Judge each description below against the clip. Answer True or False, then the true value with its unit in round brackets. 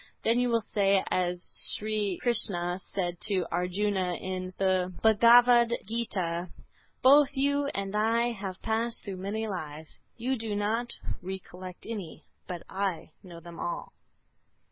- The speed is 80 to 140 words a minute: True (135 wpm)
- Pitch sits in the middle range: False (200 Hz)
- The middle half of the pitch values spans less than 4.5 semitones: True (4.0 semitones)